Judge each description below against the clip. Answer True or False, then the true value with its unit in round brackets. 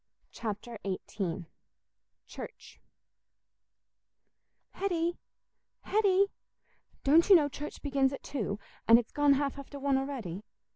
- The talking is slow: True (105 wpm)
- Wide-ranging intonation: False (5.0 semitones)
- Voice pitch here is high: True (275 Hz)